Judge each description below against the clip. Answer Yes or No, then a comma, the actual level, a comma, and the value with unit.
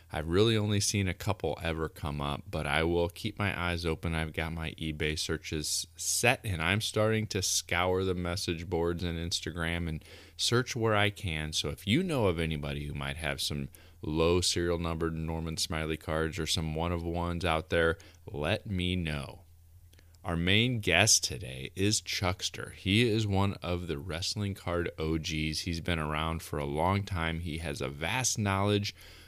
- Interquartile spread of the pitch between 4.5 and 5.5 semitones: No, average, 3.3 semitones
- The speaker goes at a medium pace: Yes, average, 180 wpm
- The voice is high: No, very low, 85 Hz